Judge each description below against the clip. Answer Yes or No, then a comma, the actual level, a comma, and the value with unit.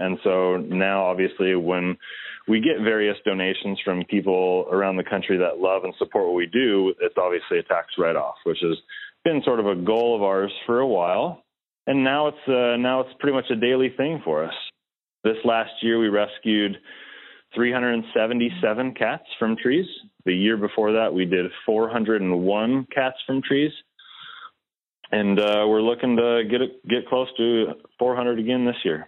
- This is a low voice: Yes, low, 115 Hz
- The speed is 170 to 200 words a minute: Yes, average, 175 wpm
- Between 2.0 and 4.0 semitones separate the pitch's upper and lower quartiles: No, average, 4.5 semitones